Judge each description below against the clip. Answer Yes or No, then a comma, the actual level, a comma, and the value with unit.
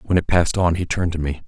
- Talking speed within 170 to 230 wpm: No, fast, 325 wpm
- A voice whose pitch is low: Yes, very low, 85 Hz